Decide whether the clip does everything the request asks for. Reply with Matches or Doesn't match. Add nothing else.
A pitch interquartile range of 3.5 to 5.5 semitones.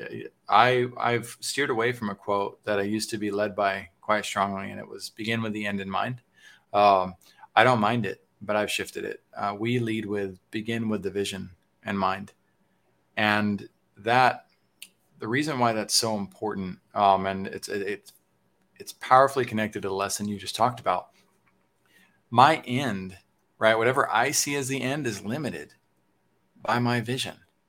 Doesn't match